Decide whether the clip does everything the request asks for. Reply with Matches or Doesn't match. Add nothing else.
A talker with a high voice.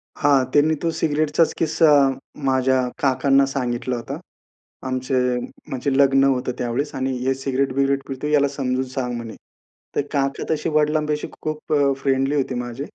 Doesn't match